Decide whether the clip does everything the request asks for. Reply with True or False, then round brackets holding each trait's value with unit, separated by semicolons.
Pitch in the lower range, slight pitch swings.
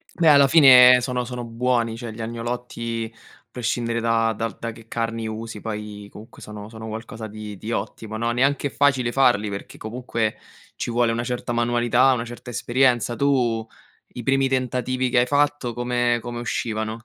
True (120 Hz; 1.9 semitones)